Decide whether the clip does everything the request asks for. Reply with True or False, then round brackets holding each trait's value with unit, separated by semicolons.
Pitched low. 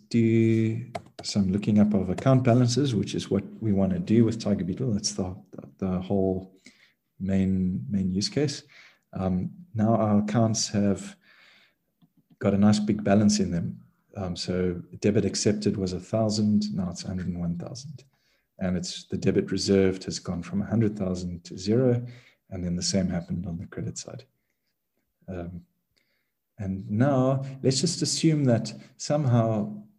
True (105 Hz)